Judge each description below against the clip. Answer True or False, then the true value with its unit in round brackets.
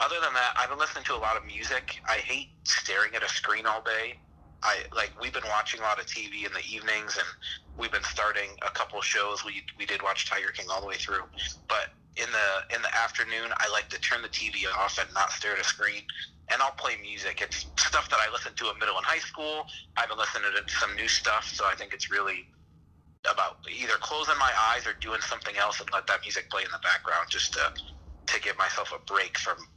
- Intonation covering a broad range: True (5.9 semitones)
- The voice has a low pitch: True (80 Hz)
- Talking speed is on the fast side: True (240 wpm)